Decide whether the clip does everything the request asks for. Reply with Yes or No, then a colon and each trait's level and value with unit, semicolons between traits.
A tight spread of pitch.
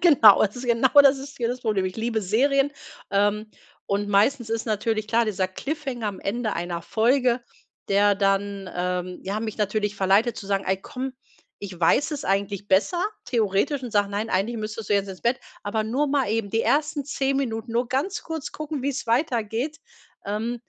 No: average, 4.4 semitones